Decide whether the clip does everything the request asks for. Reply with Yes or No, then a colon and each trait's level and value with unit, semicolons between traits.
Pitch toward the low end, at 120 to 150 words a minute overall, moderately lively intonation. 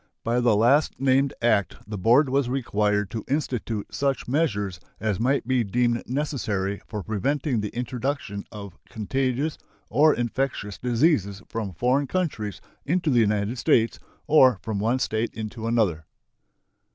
Yes: low, 120 Hz; average, 140 wpm; average, 4.4 semitones